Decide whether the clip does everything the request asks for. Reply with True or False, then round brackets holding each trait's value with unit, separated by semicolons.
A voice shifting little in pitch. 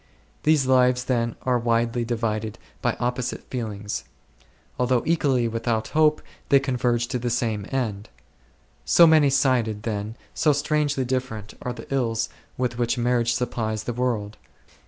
True (2.3 semitones)